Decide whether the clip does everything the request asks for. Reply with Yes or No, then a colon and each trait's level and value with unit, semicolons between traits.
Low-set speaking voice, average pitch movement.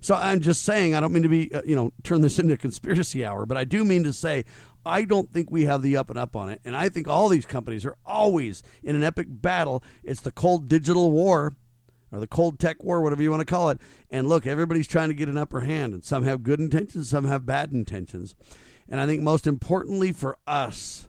No: medium, 150 Hz; average, 4.2 semitones